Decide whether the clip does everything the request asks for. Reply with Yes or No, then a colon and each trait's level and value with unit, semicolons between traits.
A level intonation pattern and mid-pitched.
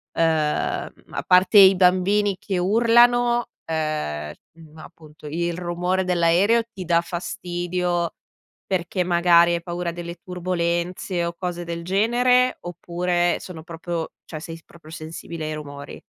Yes: narrow, 1.8 semitones; medium, 175 Hz